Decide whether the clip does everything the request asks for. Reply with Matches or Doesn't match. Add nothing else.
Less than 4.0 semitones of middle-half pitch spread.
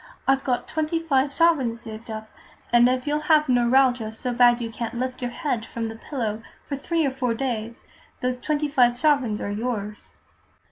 Matches